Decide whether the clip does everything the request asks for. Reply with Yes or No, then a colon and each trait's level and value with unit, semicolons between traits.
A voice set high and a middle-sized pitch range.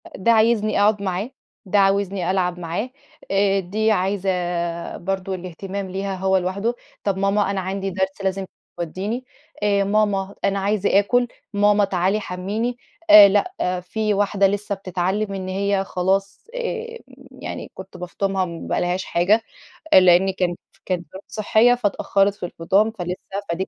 No: high, 195 Hz; narrow, 1.8 semitones